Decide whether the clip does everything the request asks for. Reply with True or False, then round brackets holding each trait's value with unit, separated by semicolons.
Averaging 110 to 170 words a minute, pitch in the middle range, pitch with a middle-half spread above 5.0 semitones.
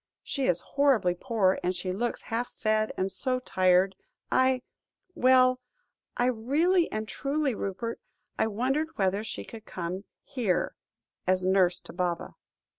False (140 wpm; 220 Hz; 5.5 semitones)